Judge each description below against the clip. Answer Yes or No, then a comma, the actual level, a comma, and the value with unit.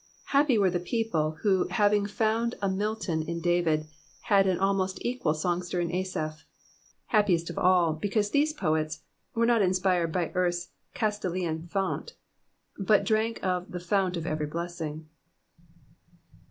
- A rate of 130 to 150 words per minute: Yes, average, 140 wpm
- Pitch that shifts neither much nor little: Yes, average, 3.6 semitones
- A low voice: No, medium, 185 Hz